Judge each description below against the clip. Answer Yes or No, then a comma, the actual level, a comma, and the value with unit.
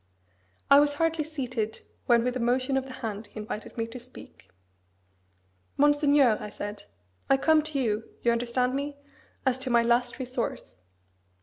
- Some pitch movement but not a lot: Yes, average, 3.2 semitones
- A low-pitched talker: No, very high, 250 Hz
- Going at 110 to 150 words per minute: No, average, 165 wpm